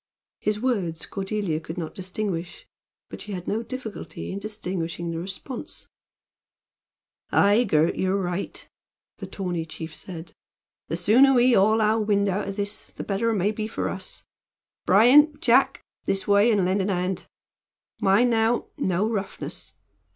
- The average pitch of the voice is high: Yes, high, 200 Hz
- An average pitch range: Yes, average, 3.4 semitones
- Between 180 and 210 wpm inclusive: No, average, 150 wpm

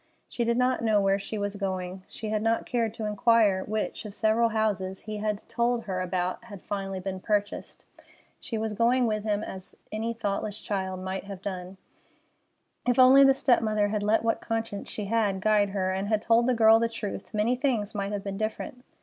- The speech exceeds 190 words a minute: Yes, fast, 205 wpm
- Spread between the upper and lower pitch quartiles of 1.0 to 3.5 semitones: Yes, narrow, 2.5 semitones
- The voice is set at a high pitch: Yes, high, 210 Hz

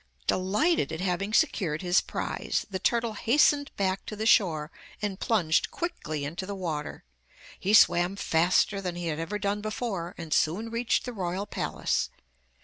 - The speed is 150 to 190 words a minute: Yes, average, 160 wpm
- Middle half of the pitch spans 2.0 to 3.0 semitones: No, average, 3.9 semitones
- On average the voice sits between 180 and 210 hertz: Yes, high, 190 Hz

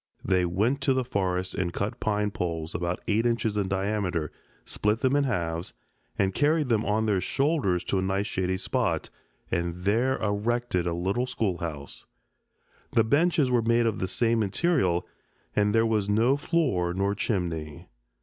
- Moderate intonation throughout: Yes, average, 4.7 semitones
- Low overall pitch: Yes, low, 105 Hz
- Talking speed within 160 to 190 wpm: Yes, average, 165 wpm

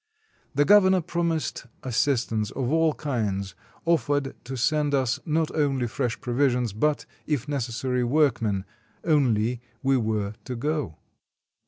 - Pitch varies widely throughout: No, average, 4.3 semitones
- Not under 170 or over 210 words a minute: No, slow, 135 wpm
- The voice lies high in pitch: No, low, 130 Hz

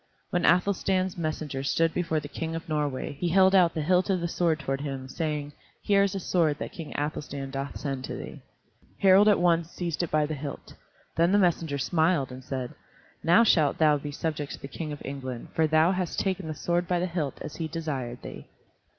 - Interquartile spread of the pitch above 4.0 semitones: No, average, 3.6 semitones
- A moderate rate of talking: No, fast, 215 wpm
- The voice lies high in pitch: No, medium, 160 Hz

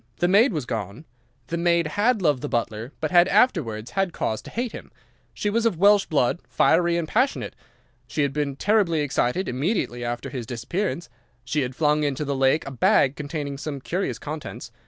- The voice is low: No, medium, 150 Hz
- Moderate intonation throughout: No, wide, 5.7 semitones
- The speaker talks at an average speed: Yes, average, 190 wpm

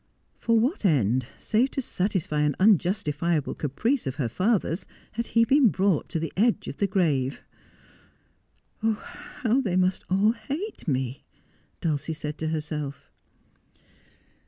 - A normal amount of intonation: No, wide, 7.2 semitones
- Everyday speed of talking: Yes, average, 145 wpm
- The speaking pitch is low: No, medium, 185 Hz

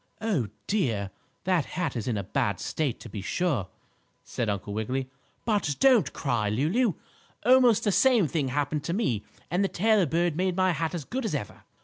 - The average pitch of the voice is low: No, medium, 160 Hz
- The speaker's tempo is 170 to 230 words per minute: Yes, average, 190 wpm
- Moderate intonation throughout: No, wide, 8.7 semitones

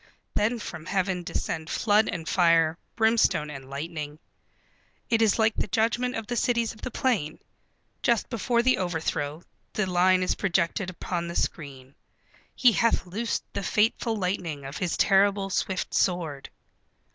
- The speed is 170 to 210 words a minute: No, average, 150 wpm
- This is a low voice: No, medium, 185 Hz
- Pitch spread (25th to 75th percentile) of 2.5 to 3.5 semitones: No, average, 5.2 semitones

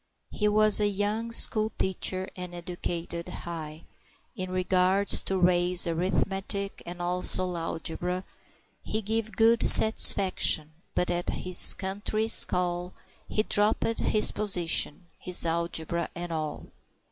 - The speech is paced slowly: Yes, slow, 120 wpm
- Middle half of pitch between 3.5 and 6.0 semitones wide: No, average, 2.9 semitones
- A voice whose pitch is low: No, medium, 180 Hz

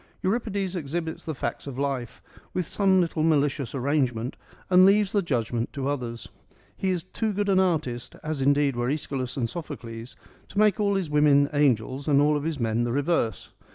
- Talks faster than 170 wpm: Yes, average, 180 wpm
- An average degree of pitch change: No, wide, 5.8 semitones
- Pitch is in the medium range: Yes, medium, 145 Hz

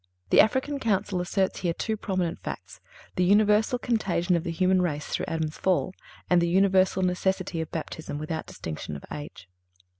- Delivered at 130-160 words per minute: No, average, 170 wpm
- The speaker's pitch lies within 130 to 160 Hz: No, medium, 185 Hz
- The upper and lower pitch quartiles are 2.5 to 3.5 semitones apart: Yes, average, 3.2 semitones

